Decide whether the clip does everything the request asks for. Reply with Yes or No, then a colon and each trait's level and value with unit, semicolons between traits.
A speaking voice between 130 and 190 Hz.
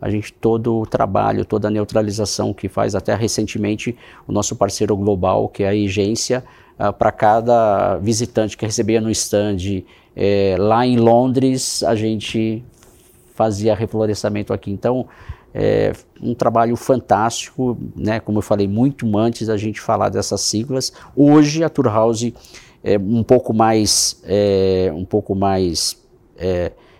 No: low, 110 Hz